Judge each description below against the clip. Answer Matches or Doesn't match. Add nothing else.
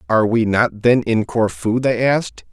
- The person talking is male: Matches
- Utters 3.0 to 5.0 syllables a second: Matches